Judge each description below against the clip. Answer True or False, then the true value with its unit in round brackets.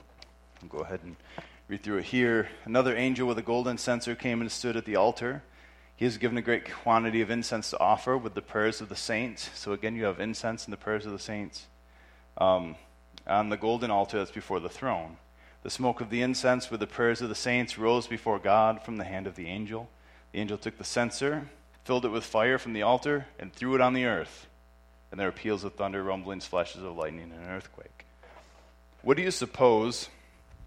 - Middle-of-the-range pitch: False (110 Hz)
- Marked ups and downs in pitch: True (6.5 semitones)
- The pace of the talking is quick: True (215 wpm)